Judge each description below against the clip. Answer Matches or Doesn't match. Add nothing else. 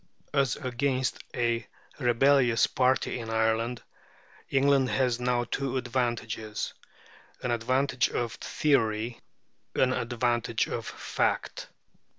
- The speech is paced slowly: Matches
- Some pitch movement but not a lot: Doesn't match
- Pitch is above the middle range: Doesn't match